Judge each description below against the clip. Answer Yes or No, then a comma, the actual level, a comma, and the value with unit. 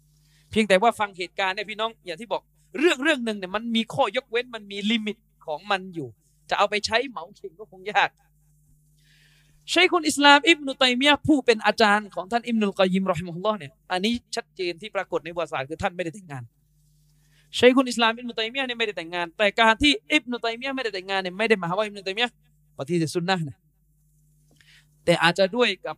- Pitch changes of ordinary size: No, wide, 6.6 semitones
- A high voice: Yes, high, 195 Hz